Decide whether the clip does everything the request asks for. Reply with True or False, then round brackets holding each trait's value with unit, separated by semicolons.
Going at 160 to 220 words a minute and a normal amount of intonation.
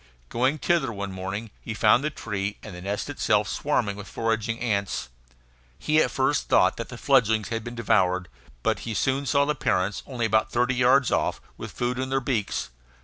True (195 wpm; 4.4 semitones)